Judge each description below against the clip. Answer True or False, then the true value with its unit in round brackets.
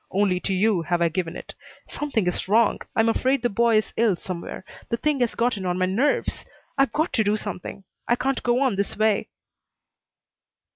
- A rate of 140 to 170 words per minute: False (195 wpm)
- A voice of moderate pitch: False (215 Hz)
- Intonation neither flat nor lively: True (4.4 semitones)